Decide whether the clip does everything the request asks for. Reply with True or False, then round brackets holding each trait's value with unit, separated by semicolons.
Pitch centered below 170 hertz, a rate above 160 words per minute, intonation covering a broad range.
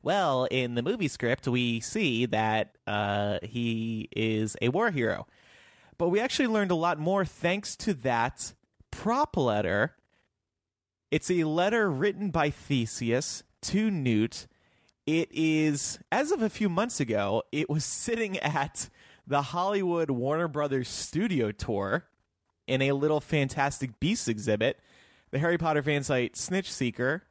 False (135 Hz; 140 wpm; 7.0 semitones)